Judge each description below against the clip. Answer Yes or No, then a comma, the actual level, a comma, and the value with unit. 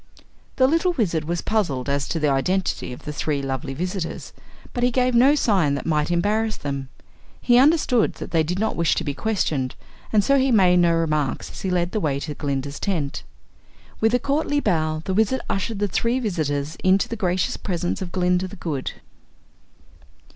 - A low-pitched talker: No, medium, 180 Hz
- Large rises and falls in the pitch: Yes, wide, 6.5 semitones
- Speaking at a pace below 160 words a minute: No, average, 190 wpm